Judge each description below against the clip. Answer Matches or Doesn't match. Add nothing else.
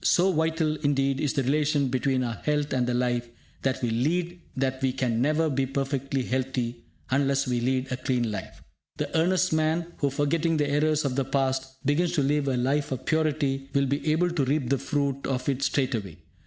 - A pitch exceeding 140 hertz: Doesn't match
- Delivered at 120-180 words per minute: Doesn't match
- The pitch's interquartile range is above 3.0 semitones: Doesn't match